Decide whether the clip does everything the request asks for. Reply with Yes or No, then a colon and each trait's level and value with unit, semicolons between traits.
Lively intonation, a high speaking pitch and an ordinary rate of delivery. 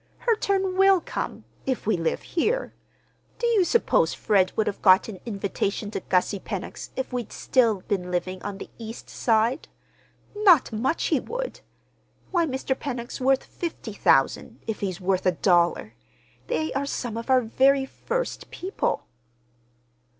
Yes: wide, 8.6 semitones; high, 230 Hz; average, 150 wpm